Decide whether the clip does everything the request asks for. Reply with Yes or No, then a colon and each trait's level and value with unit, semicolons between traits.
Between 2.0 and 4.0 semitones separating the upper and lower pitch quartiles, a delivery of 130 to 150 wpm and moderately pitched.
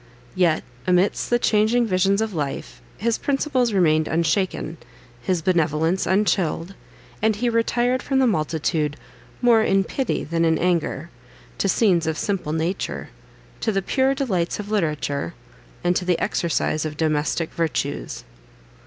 No: average, 5.2 semitones; average, 140 wpm; medium, 180 Hz